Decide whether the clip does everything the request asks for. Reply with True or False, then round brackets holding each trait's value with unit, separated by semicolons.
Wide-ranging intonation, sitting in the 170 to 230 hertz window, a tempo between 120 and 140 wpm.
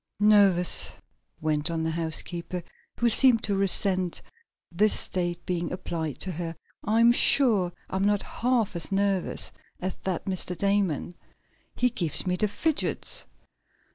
False (3.2 semitones; 185 Hz; 135 wpm)